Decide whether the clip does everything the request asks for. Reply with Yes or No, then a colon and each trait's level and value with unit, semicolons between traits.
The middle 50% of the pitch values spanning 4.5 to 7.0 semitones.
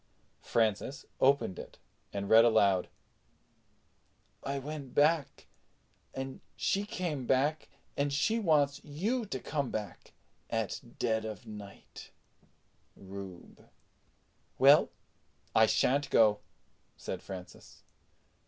Yes: average, 5.3 semitones